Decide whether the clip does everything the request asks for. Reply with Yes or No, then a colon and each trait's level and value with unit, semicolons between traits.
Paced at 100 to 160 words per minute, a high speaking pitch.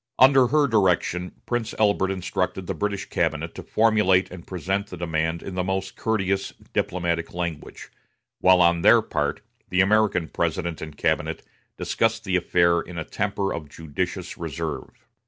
No: average, 155 wpm; very low, 95 Hz